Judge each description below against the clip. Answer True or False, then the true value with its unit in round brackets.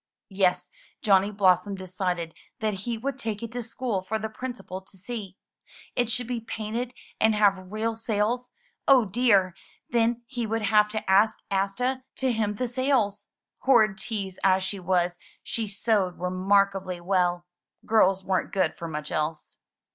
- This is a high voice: True (210 Hz)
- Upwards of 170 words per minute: False (155 wpm)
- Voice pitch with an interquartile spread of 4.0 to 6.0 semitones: False (3.4 semitones)